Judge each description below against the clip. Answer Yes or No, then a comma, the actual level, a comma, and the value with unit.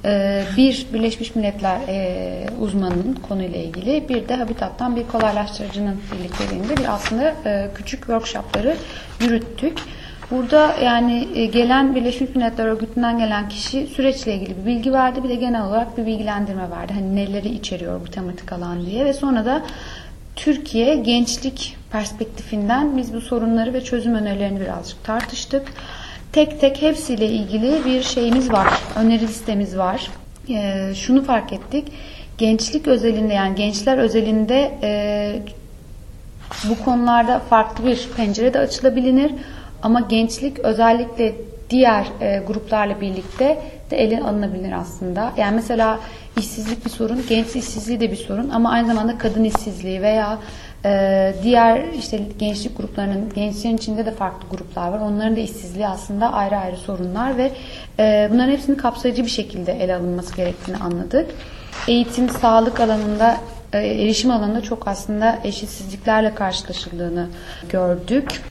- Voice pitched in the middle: No, high, 225 Hz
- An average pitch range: Yes, average, 3.2 semitones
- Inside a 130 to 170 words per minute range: Yes, average, 135 wpm